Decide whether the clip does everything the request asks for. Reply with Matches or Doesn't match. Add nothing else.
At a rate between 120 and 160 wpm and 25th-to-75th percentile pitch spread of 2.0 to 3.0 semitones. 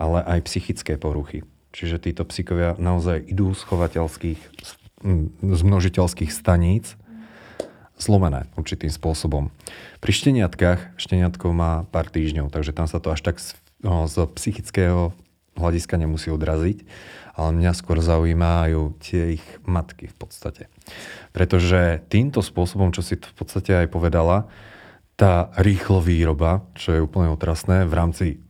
Matches